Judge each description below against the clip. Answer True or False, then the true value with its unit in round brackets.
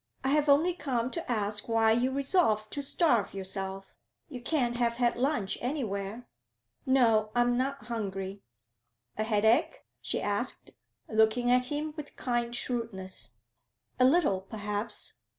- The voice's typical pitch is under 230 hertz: False (240 Hz)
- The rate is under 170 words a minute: True (140 wpm)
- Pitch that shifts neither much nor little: True (4.1 semitones)